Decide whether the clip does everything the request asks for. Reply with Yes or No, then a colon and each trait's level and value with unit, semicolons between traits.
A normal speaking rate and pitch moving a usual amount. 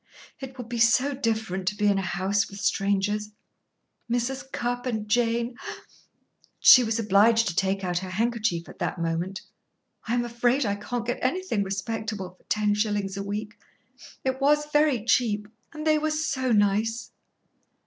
Yes: average, 170 wpm; average, 3.4 semitones